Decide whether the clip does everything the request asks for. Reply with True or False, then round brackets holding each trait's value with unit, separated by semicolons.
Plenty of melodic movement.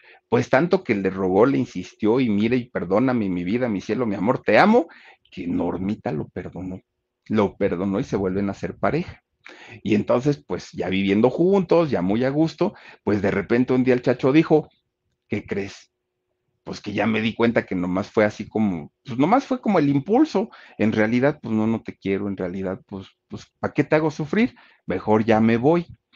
True (7.1 semitones)